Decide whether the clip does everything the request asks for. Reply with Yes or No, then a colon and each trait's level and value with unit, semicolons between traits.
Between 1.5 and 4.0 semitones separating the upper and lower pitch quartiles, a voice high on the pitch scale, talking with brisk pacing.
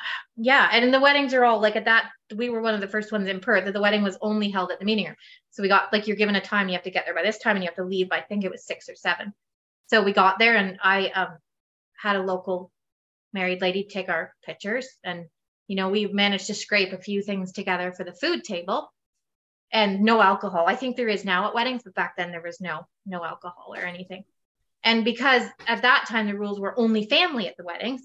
Yes: average, 3.4 semitones; high, 205 Hz; fast, 260 wpm